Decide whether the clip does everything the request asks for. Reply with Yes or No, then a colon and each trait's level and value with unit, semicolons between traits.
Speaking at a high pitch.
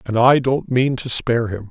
No: low, 120 Hz